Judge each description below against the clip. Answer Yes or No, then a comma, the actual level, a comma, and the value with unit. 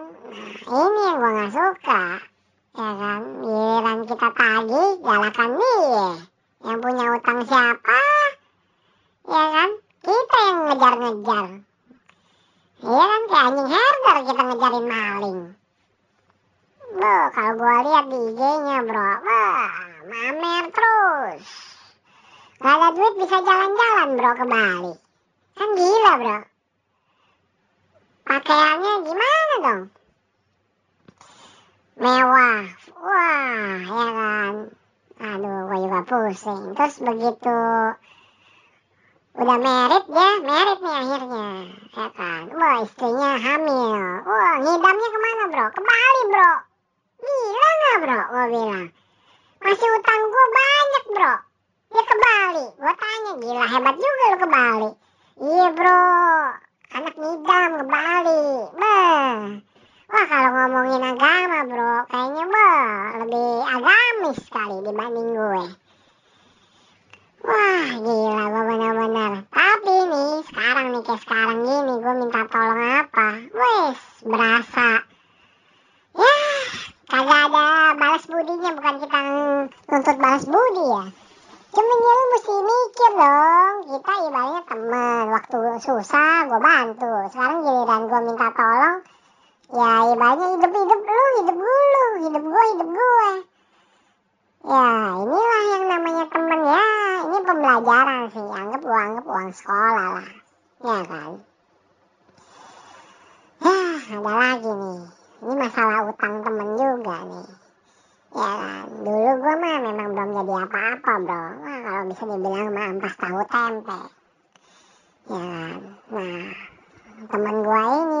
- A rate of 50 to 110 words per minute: No, average, 120 wpm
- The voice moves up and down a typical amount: No, wide, 7.7 semitones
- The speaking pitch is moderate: No, very high, 260 Hz